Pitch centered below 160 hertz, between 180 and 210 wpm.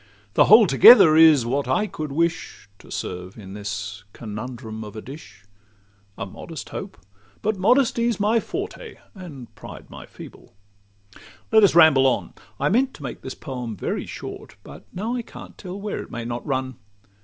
No: low, 135 Hz; average, 165 wpm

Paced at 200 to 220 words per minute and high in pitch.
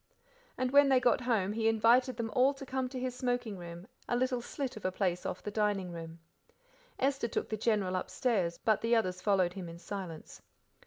Yes: fast, 205 wpm; high, 220 Hz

